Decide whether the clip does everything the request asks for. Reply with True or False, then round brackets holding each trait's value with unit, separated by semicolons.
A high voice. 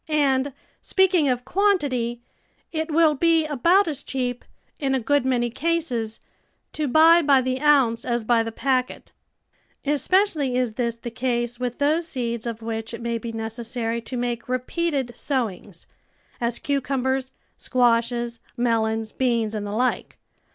True (250 Hz)